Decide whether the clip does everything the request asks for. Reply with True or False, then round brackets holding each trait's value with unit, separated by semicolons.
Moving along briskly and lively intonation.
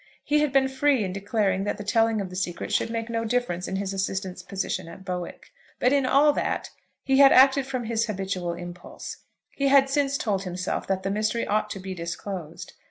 True (210 wpm; 5.7 semitones)